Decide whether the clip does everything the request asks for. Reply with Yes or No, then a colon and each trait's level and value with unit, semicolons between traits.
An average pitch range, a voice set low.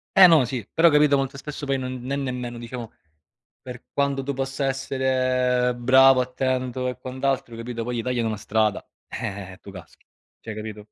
No: narrow, 2.3 semitones; low, 125 Hz